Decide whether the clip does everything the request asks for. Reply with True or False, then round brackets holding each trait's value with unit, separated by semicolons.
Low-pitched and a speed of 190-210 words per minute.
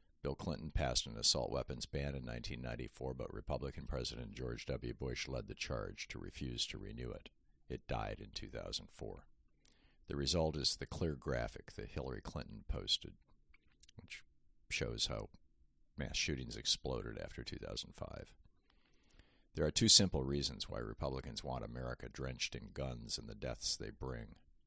False (70 Hz; 150 wpm)